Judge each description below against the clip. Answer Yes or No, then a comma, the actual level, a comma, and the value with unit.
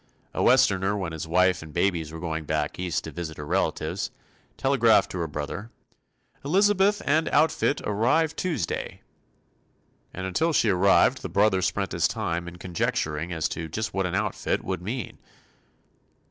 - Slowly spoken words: No, average, 160 wpm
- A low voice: Yes, very low, 95 Hz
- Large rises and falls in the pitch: Yes, wide, 6.0 semitones